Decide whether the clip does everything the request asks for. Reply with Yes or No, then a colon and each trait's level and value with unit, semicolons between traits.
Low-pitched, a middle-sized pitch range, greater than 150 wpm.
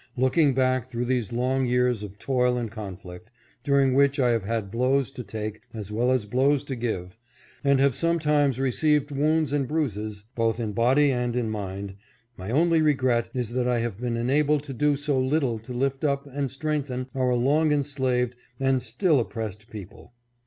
Yes: low, 125 Hz; average, 3.4 semitones; average, 180 wpm